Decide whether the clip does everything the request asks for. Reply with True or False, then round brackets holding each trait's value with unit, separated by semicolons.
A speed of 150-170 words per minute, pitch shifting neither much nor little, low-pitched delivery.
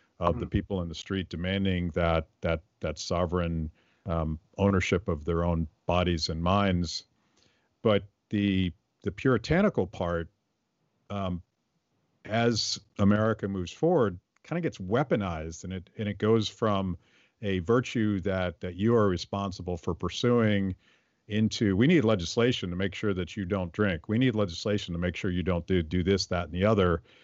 True (165 wpm; 3.1 semitones; 95 Hz)